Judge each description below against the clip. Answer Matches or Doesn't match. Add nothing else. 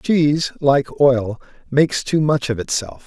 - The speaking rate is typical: Matches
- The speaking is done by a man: Matches